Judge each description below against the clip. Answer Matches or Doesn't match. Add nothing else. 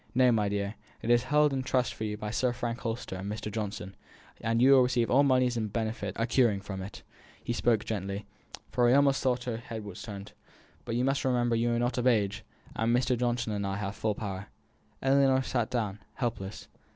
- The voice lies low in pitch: Matches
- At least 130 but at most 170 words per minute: Doesn't match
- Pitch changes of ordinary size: Matches